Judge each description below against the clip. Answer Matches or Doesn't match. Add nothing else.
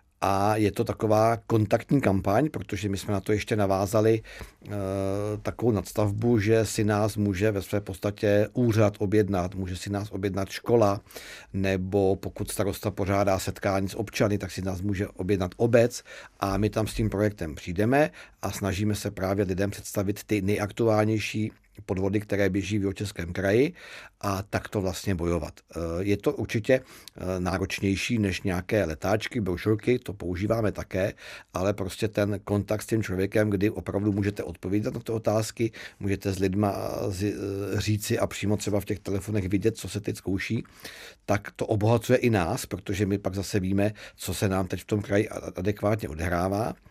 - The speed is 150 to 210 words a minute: Matches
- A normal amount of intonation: Doesn't match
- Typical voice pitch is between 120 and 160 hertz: Doesn't match